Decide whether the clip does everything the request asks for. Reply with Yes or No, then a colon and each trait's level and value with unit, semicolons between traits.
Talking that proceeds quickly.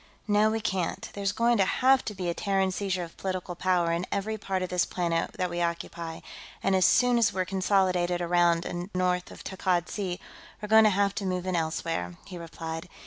Yes: fast, 210 wpm